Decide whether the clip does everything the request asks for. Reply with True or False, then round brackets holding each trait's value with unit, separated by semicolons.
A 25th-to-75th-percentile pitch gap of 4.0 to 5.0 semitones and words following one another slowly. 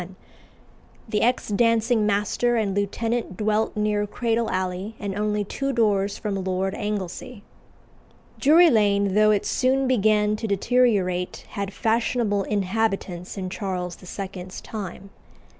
False (2.6 semitones; 125 wpm)